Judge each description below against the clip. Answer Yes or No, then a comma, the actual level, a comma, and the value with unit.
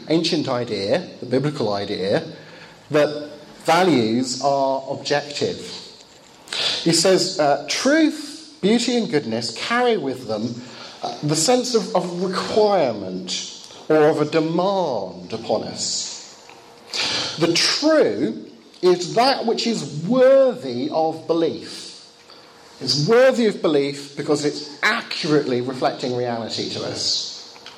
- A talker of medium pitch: Yes, medium, 155 Hz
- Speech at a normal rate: No, slow, 110 wpm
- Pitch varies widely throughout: Yes, wide, 7.3 semitones